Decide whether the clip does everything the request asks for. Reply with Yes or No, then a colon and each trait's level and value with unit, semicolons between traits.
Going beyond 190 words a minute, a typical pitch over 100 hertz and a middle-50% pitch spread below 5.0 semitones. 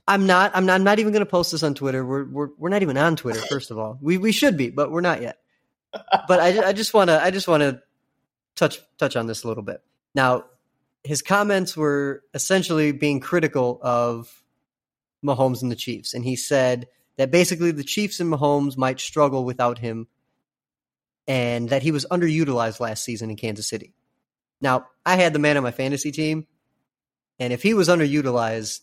No: average, 200 wpm; medium, 140 Hz; average, 5.3 semitones